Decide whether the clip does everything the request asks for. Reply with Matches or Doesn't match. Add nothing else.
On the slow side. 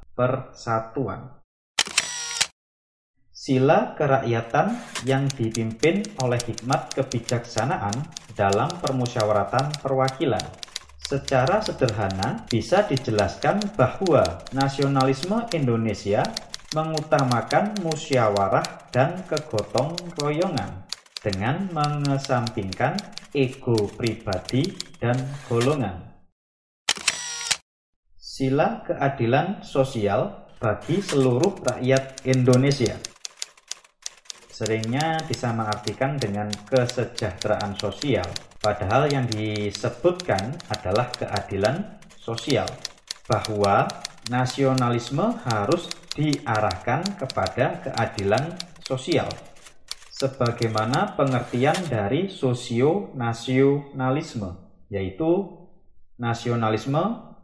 Matches